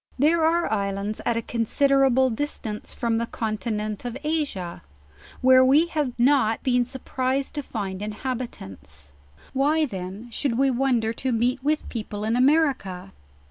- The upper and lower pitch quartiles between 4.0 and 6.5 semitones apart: Yes, average, 4.3 semitones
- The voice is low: No, high, 245 Hz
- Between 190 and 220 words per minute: No, average, 150 wpm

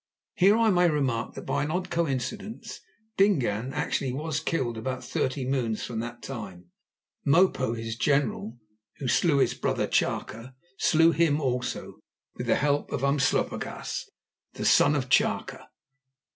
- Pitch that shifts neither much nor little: Yes, average, 4.8 semitones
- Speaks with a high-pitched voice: No, low, 135 Hz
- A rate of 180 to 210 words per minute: No, average, 145 wpm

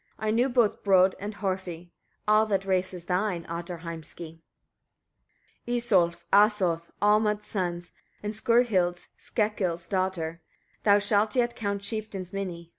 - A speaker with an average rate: No, slow, 130 wpm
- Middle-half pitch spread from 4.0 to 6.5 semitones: No, average, 3.4 semitones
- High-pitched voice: Yes, high, 195 Hz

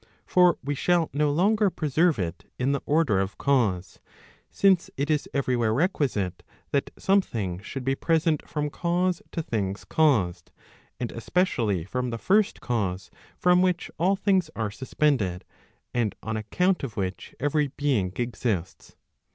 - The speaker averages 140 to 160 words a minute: Yes, average, 150 wpm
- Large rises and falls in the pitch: Yes, wide, 7.8 semitones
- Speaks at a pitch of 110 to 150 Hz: Yes, medium, 140 Hz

